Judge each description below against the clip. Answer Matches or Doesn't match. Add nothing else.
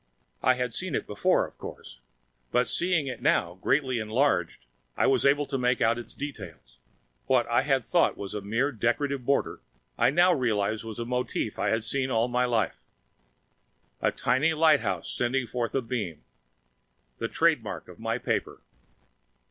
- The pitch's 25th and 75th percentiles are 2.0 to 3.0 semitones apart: Doesn't match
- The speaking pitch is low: Matches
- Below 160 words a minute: Doesn't match